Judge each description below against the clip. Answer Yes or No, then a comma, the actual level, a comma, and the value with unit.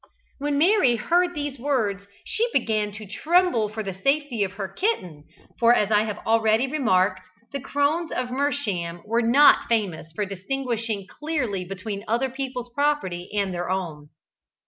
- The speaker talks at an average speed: Yes, average, 155 wpm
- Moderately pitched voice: No, high, 225 Hz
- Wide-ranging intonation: Yes, wide, 6.2 semitones